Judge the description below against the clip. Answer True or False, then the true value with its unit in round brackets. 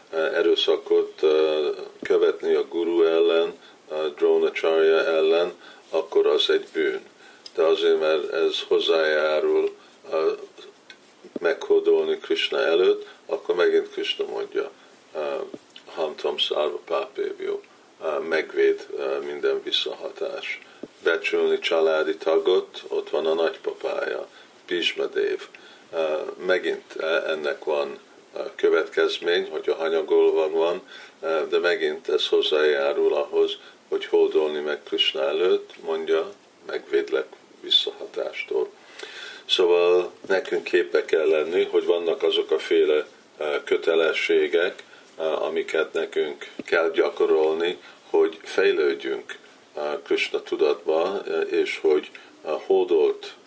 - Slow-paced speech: True (90 wpm)